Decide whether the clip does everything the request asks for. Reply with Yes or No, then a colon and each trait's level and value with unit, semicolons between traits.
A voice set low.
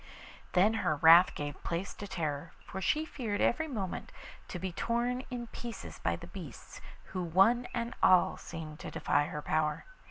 No: high, 190 Hz